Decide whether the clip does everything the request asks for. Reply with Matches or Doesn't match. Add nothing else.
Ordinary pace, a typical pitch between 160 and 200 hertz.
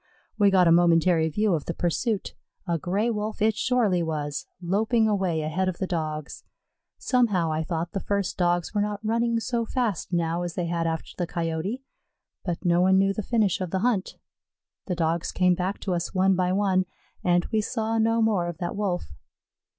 Matches